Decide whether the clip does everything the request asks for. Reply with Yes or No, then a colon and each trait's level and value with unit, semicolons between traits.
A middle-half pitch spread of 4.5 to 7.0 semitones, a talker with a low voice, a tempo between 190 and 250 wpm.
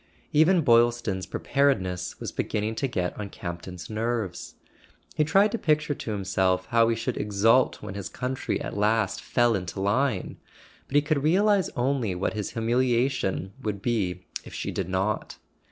No: wide, 5.6 semitones; low, 115 Hz; average, 160 wpm